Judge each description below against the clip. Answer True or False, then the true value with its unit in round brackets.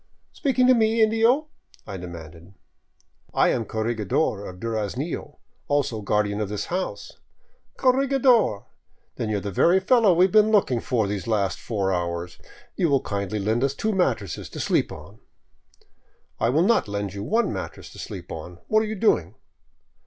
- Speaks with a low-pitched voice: True (115 Hz)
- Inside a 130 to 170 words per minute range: False (180 wpm)